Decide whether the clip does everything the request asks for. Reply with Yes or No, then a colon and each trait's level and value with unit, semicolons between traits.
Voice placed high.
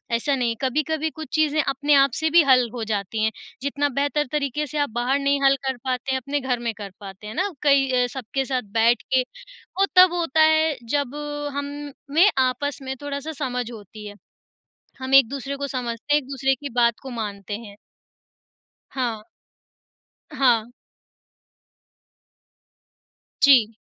Yes: very high, 270 Hz